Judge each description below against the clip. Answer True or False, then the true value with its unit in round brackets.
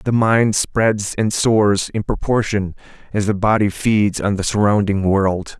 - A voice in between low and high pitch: False (105 Hz)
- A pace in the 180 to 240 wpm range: False (160 wpm)